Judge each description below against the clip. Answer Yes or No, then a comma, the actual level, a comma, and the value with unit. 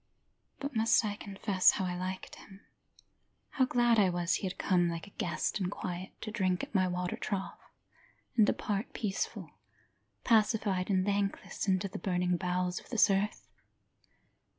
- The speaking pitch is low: No, high, 195 Hz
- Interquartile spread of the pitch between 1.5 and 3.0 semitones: Yes, narrow, 2.5 semitones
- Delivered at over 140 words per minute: Yes, average, 160 wpm